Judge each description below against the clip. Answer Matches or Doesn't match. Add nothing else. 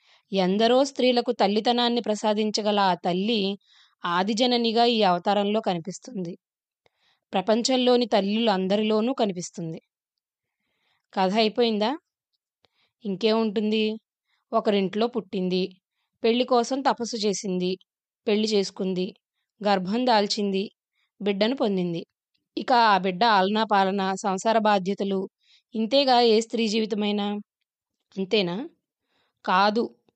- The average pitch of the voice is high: Matches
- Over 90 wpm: Doesn't match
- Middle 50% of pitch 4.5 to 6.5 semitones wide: Doesn't match